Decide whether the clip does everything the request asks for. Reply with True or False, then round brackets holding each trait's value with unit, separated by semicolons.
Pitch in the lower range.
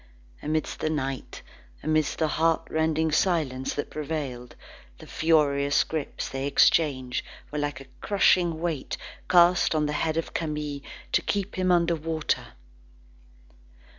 False (155 Hz)